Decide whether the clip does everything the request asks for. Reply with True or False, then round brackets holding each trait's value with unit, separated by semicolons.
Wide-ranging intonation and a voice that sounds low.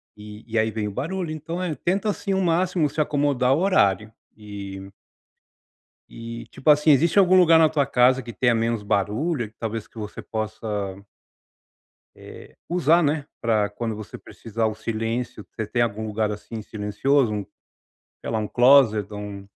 True (6.0 semitones; 115 Hz)